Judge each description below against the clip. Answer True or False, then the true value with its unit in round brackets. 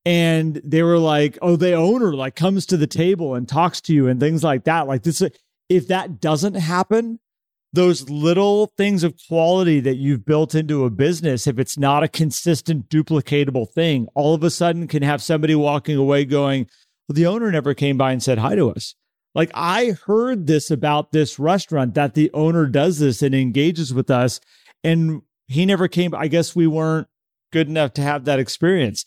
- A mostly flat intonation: False (3.2 semitones)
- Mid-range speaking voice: True (155 Hz)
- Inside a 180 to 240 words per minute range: True (195 wpm)